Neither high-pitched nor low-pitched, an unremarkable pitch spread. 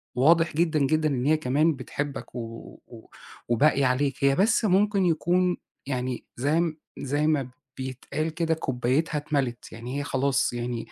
Yes: medium, 145 Hz; average, 3.9 semitones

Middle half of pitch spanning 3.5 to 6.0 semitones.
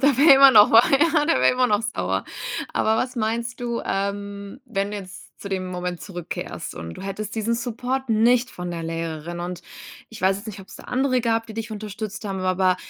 Yes: average, 4.3 semitones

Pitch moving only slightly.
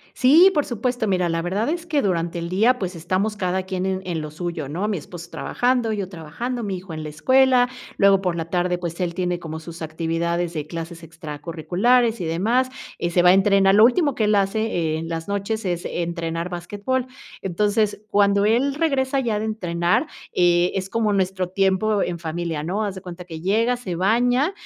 No: average, 4.4 semitones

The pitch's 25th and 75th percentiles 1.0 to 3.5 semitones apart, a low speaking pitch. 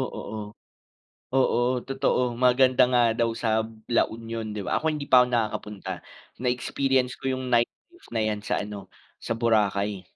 Yes: average, 2.8 semitones; low, 120 Hz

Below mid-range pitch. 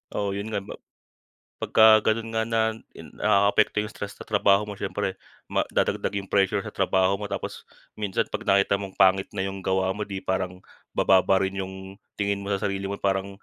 Yes: low, 100 Hz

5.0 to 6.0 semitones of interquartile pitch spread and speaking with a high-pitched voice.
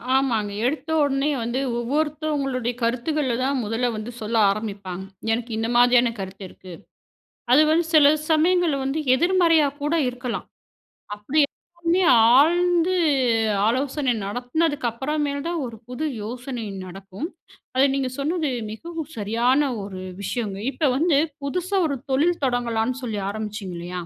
Yes: wide, 5.4 semitones; very high, 260 Hz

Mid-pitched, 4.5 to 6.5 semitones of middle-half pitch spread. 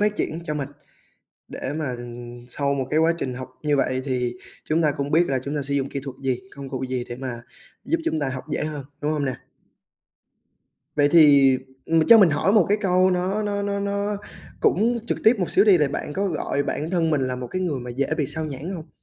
Yes: medium, 150 Hz; average, 5.2 semitones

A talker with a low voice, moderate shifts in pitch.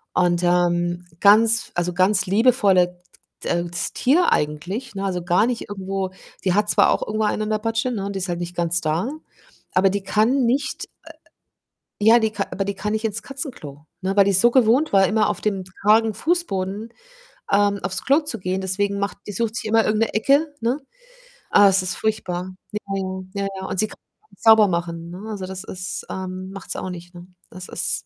No: high, 200 Hz; average, 3.2 semitones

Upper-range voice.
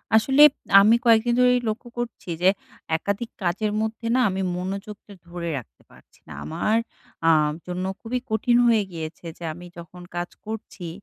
Yes: high, 205 Hz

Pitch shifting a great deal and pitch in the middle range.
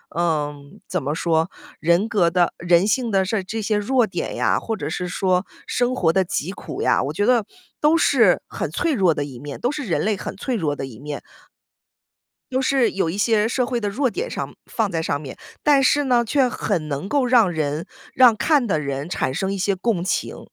No: wide, 6.9 semitones; high, 195 Hz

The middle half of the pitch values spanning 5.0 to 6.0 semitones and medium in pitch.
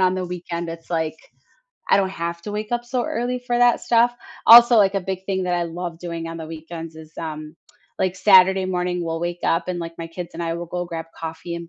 No: narrow, 2.5 semitones; medium, 175 Hz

